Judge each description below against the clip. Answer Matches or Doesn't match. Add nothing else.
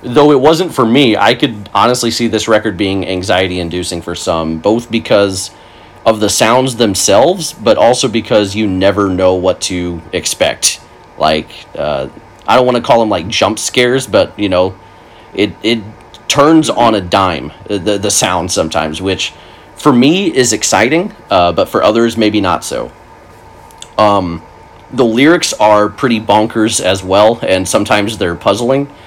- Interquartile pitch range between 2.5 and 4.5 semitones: Matches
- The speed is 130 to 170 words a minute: Matches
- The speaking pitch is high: Doesn't match